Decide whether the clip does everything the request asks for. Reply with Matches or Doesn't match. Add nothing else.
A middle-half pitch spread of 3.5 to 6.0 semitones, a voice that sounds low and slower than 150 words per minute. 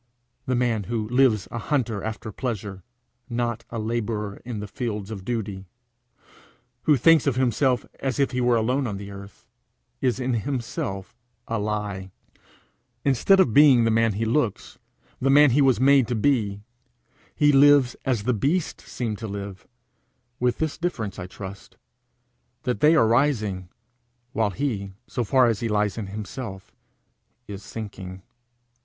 Doesn't match